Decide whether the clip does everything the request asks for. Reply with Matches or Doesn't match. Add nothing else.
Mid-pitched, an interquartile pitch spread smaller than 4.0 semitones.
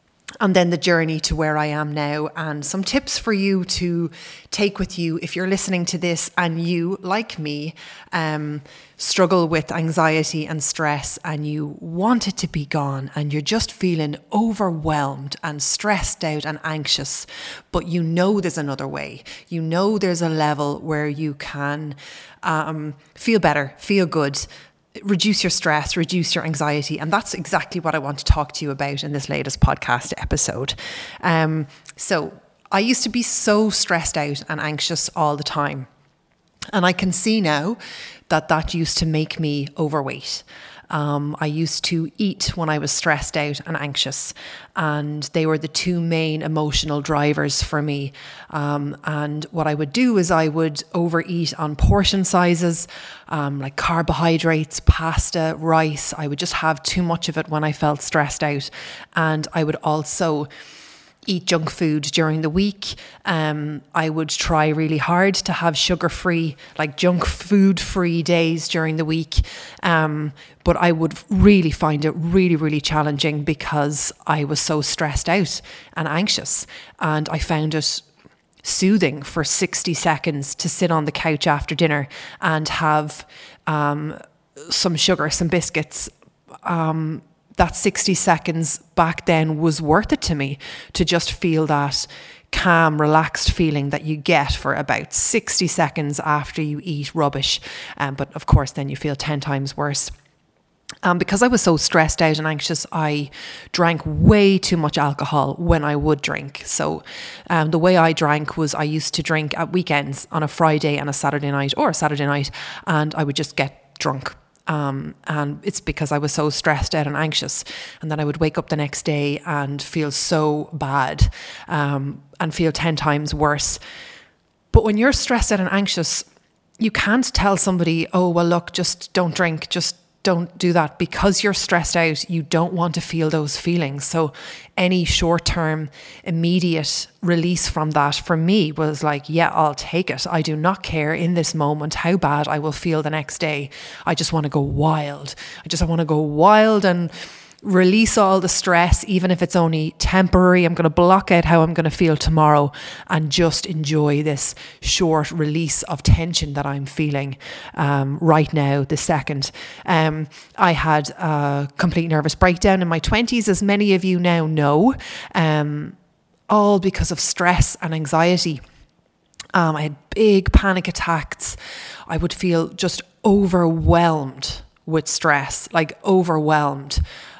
Matches